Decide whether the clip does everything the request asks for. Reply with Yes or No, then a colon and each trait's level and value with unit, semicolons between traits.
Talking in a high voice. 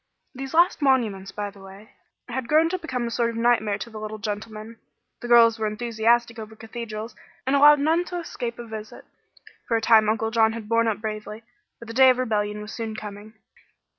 Yes: high, 225 Hz